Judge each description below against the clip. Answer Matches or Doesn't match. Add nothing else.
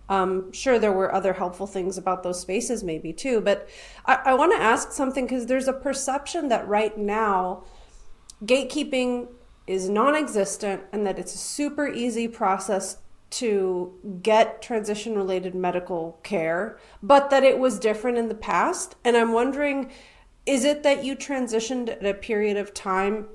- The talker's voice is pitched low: Doesn't match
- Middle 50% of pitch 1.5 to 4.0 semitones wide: Doesn't match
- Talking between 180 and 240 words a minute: Doesn't match